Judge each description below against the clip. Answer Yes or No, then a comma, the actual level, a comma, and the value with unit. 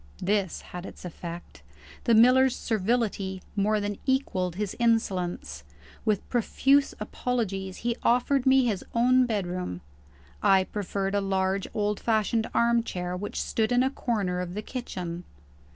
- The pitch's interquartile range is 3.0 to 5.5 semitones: Yes, average, 4.0 semitones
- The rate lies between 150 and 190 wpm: No, slow, 135 wpm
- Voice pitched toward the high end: Yes, high, 210 Hz